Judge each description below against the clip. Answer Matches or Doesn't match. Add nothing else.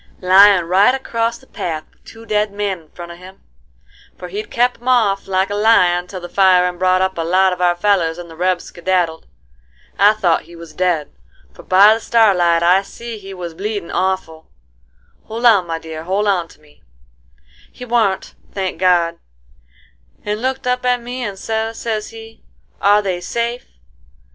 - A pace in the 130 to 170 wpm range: Doesn't match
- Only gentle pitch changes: Doesn't match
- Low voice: Doesn't match